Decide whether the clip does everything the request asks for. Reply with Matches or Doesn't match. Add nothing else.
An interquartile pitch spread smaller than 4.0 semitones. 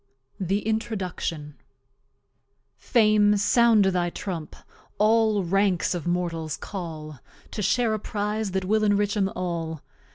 Matches